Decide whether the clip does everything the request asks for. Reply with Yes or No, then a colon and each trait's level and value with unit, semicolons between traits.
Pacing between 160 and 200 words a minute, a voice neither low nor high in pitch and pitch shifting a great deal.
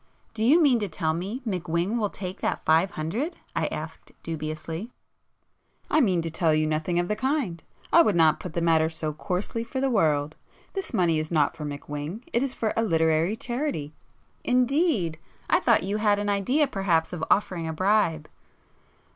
Yes: average, 180 wpm; medium, 180 Hz; wide, 6.0 semitones